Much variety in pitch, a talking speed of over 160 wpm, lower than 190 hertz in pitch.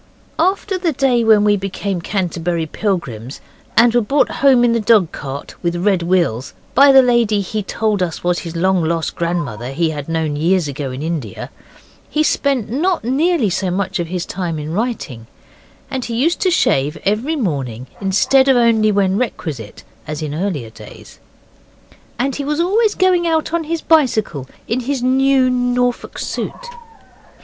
No: wide, 7.9 semitones; average, 170 wpm; high, 205 Hz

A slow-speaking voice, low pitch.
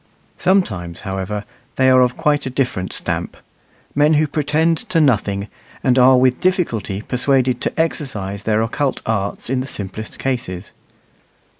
No: average, 145 wpm; low, 125 Hz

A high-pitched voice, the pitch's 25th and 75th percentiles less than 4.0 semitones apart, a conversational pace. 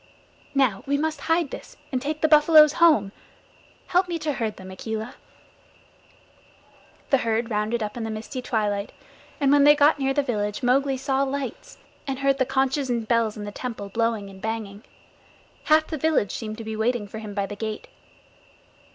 No: high, 245 Hz; average, 4.6 semitones; average, 185 wpm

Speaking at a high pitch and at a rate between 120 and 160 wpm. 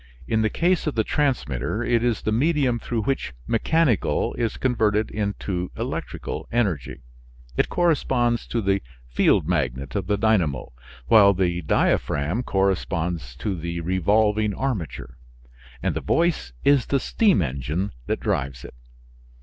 No: low, 105 Hz; average, 140 wpm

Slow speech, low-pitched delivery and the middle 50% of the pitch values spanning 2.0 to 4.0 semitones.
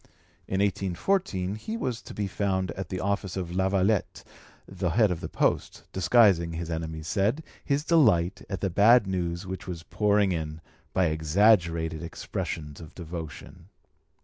No: average, 150 wpm; very low, 95 Hz; average, 3.4 semitones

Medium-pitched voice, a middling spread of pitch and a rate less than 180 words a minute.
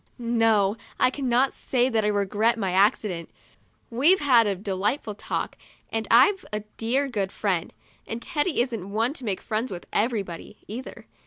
No: high, 225 Hz; average, 3.7 semitones; average, 160 wpm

